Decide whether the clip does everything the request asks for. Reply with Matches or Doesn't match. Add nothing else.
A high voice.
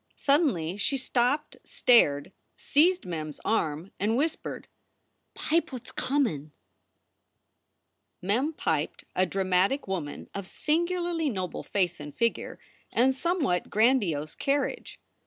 Matches